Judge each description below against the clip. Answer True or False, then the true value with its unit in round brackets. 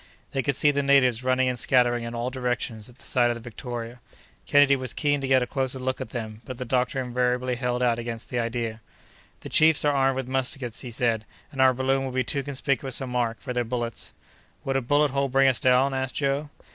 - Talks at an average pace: False (235 wpm)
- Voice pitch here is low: True (130 Hz)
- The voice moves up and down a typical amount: False (1.9 semitones)